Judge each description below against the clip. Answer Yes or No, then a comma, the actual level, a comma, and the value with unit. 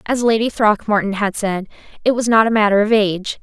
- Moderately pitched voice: No, high, 210 Hz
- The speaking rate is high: Yes, fast, 210 wpm